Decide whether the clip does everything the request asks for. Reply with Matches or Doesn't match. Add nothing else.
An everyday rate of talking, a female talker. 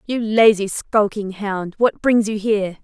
Matches